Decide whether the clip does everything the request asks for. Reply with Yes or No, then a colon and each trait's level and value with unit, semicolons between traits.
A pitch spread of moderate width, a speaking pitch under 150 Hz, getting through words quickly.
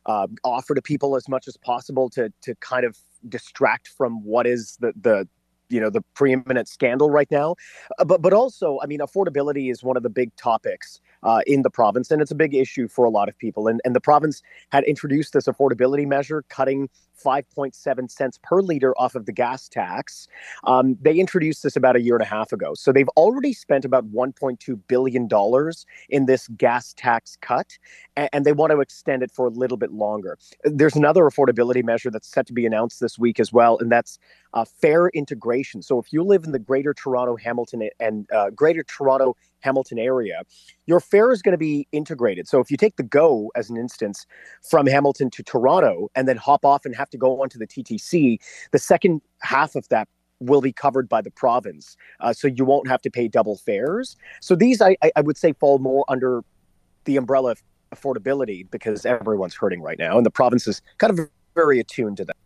Yes: average, 3.4 semitones; low, 135 Hz; fast, 210 wpm